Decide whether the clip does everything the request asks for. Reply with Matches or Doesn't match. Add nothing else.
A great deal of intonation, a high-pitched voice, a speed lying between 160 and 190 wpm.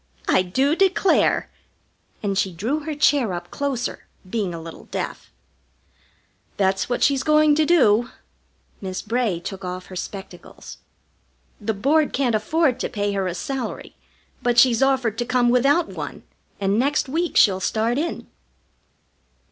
Doesn't match